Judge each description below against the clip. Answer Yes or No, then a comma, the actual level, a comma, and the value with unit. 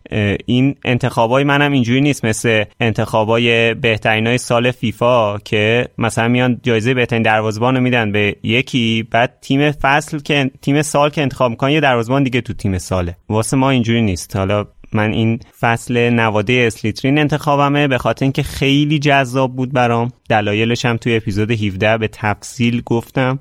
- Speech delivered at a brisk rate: Yes, fast, 160 wpm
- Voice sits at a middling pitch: No, low, 120 Hz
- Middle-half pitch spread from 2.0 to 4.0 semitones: Yes, average, 3.2 semitones